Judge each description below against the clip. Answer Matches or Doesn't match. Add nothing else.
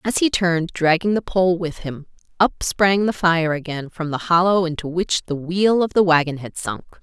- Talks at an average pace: Doesn't match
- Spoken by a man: Doesn't match